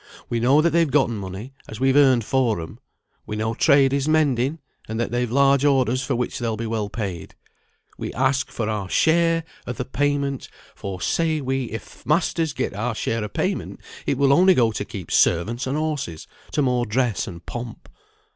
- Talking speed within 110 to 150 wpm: No, average, 195 wpm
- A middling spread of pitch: Yes, average, 4.1 semitones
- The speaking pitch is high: No, low, 125 Hz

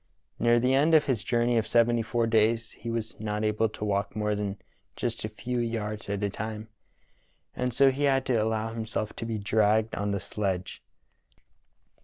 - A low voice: Yes, low, 110 Hz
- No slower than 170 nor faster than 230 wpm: Yes, average, 180 wpm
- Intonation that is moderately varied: No, narrow, 2.0 semitones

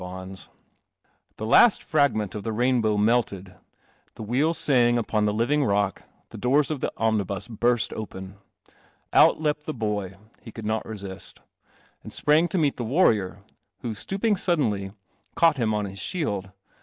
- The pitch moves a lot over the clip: Yes, wide, 5.8 semitones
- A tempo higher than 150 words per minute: No, average, 145 wpm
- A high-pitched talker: No, low, 110 Hz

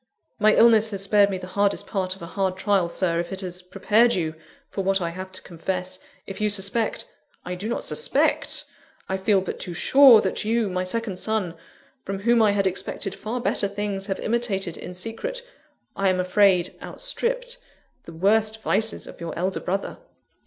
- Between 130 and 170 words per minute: No, average, 190 wpm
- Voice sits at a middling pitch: No, high, 195 Hz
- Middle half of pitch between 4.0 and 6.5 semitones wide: No, average, 3.0 semitones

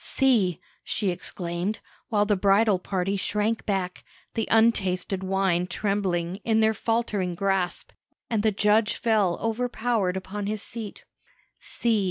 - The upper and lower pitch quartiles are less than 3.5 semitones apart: Yes, average, 2.9 semitones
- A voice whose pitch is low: No, high, 205 Hz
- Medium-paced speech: No, slow, 130 wpm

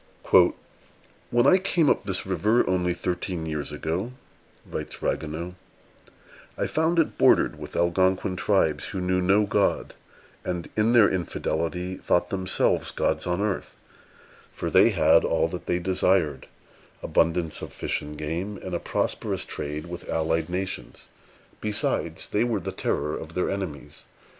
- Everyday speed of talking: Yes, average, 150 wpm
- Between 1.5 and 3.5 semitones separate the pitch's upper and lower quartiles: Yes, average, 3.2 semitones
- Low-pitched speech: Yes, very low, 90 Hz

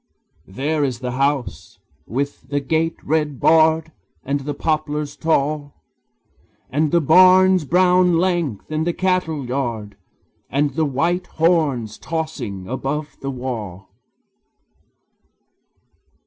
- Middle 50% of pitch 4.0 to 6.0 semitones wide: No, average, 3.5 semitones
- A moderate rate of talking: No, slow, 110 wpm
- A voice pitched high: No, medium, 150 Hz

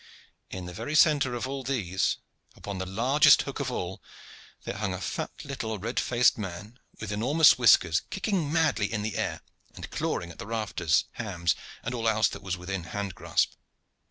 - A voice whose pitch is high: No, low, 110 Hz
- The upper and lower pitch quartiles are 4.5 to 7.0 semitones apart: Yes, wide, 5.6 semitones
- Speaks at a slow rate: No, average, 180 wpm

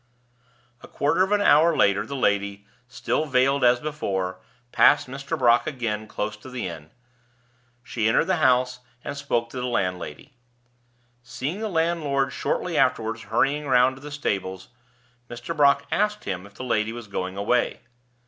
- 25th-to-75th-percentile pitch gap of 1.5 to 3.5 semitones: No, average, 5.2 semitones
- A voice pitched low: Yes, low, 125 Hz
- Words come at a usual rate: Yes, average, 160 wpm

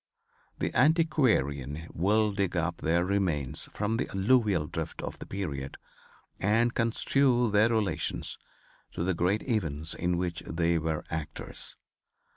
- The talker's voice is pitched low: Yes, very low, 95 Hz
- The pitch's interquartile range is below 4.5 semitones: No, wide, 5.4 semitones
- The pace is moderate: No, slow, 130 wpm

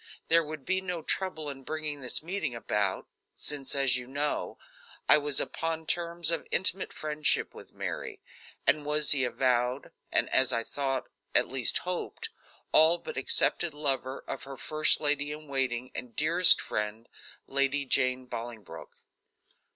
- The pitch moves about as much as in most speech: Yes, average, 3.4 semitones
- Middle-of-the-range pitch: Yes, medium, 145 Hz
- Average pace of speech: Yes, average, 150 wpm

